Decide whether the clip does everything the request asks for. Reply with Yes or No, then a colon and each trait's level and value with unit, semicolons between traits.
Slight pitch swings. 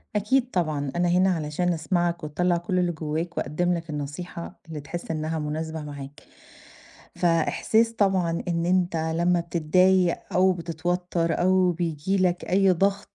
Yes: narrow, 2.3 semitones